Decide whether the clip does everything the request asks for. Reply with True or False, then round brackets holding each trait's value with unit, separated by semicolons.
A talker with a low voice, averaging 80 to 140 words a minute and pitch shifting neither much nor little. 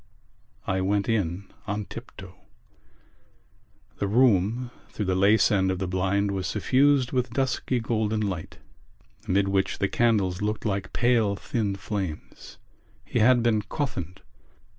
True (105 Hz; 135 wpm; 3.6 semitones)